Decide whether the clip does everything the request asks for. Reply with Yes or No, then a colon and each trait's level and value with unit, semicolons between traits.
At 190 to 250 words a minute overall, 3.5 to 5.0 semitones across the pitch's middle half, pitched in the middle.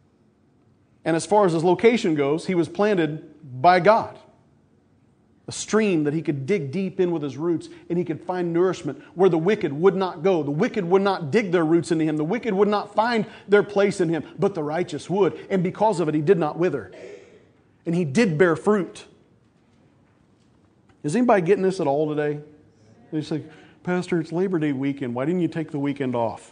Yes: fast, 205 wpm; average, 4.3 semitones; medium, 170 Hz